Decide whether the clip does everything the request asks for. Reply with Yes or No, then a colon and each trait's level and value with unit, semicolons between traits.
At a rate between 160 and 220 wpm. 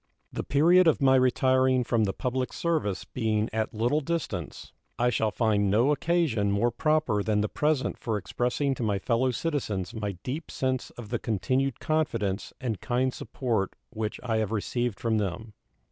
Yes: average, 170 wpm